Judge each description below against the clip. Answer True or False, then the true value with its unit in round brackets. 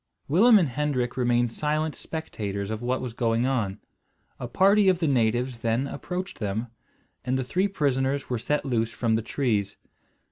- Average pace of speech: True (170 wpm)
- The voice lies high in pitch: False (125 Hz)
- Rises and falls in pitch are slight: False (4.5 semitones)